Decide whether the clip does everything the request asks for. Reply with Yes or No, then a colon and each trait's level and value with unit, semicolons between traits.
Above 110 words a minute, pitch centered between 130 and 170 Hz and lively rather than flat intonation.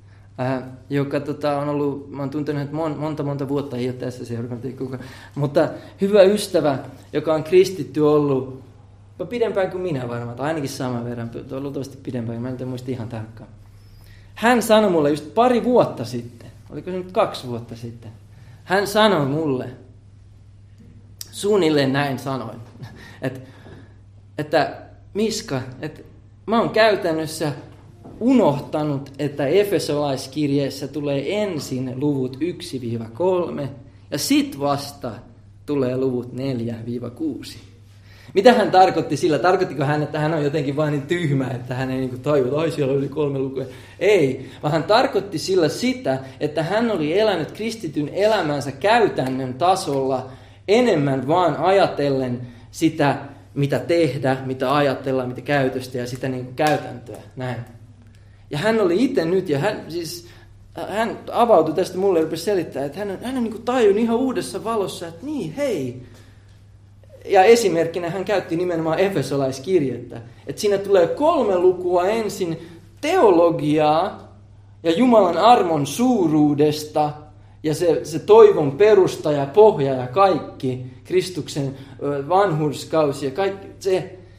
Yes: average, 135 wpm; medium, 140 Hz; wide, 5.8 semitones